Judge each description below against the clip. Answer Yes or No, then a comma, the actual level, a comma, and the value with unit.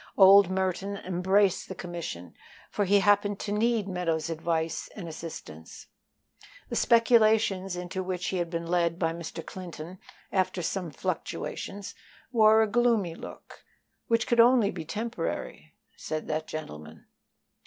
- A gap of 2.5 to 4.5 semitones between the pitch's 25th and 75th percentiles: Yes, average, 3.6 semitones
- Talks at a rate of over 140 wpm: No, slow, 135 wpm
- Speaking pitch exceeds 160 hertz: Yes, medium, 185 Hz